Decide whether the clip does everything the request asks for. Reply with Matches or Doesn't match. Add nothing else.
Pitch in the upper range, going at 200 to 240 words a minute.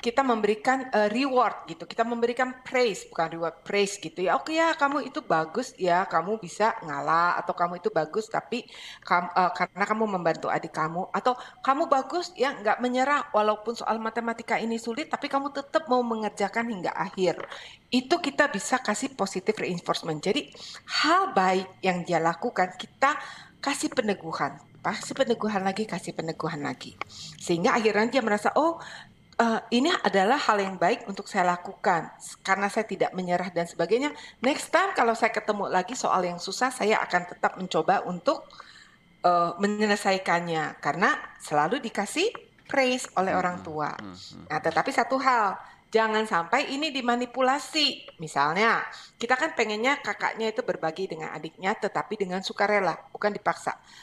Doesn't match